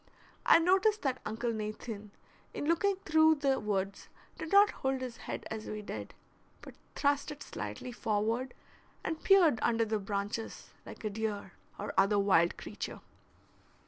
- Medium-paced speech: Yes, average, 150 wpm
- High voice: Yes, high, 230 Hz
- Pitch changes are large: Yes, wide, 6.3 semitones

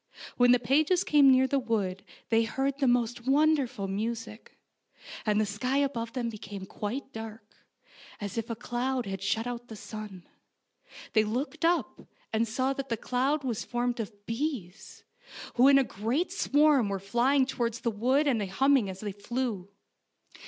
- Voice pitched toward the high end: Yes, high, 240 Hz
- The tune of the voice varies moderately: Yes, average, 4.0 semitones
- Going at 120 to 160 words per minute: No, average, 170 wpm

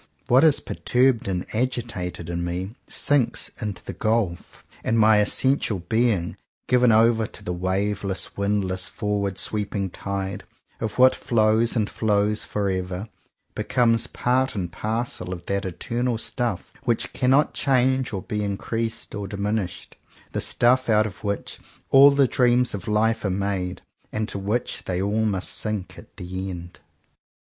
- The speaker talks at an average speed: Yes, average, 150 wpm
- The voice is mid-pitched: No, low, 105 Hz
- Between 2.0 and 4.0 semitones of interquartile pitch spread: Yes, average, 3.5 semitones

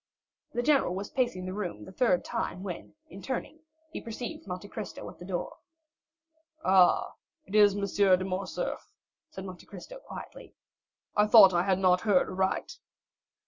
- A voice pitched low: No, high, 195 Hz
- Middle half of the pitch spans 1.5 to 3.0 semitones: Yes, narrow, 2.6 semitones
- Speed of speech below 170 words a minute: Yes, average, 160 wpm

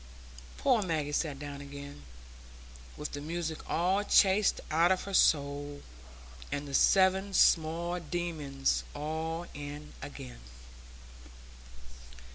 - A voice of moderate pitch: Yes, medium, 155 Hz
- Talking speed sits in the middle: No, slow, 105 wpm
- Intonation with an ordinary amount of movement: Yes, average, 3.5 semitones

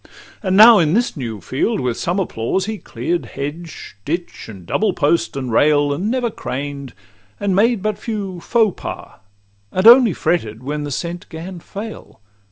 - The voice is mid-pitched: Yes, medium, 175 Hz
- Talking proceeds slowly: No, average, 170 wpm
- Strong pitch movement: Yes, wide, 6.5 semitones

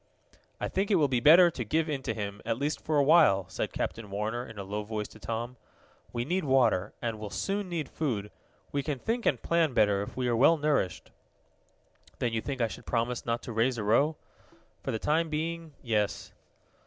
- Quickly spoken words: Yes, fast, 215 wpm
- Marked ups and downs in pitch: Yes, wide, 5.9 semitones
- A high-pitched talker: No, low, 125 Hz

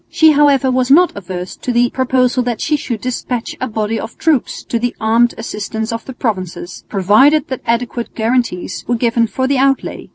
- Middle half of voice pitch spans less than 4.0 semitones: Yes, average, 2.8 semitones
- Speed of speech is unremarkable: Yes, average, 190 wpm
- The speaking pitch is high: Yes, high, 240 Hz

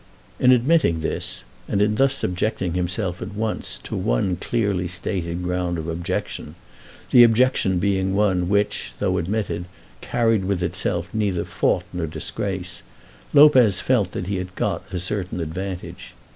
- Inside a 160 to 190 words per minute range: No, average, 145 wpm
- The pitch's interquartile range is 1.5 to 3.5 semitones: Yes, average, 3.1 semitones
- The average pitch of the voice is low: Yes, very low, 95 Hz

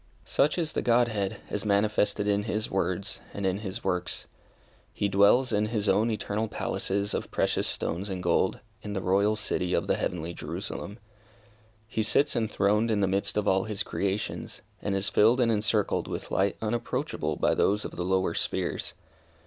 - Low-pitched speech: Yes, low, 105 Hz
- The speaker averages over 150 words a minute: Yes, average, 175 wpm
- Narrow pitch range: Yes, narrow, 2.1 semitones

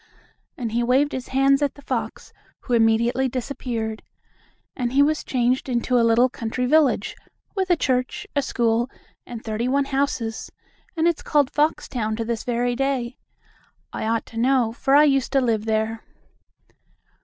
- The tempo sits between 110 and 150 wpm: No, average, 165 wpm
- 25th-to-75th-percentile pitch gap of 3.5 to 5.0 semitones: No, average, 3.1 semitones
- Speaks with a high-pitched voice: Yes, very high, 250 Hz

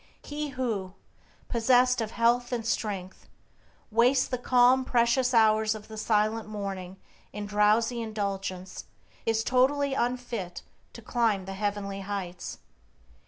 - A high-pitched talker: Yes, high, 220 Hz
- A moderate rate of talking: No, slow, 120 wpm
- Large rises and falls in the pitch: No, average, 3.3 semitones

